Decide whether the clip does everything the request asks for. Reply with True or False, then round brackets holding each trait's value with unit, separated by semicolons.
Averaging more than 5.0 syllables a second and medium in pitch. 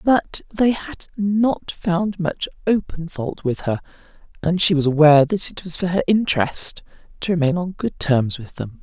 False (4.5 syllables/s; 175 Hz)